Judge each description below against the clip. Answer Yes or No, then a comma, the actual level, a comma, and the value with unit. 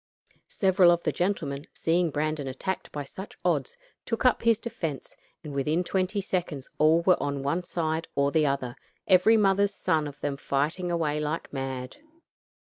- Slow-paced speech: No, average, 165 wpm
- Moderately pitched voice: Yes, medium, 160 Hz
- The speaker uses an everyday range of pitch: Yes, average, 4.6 semitones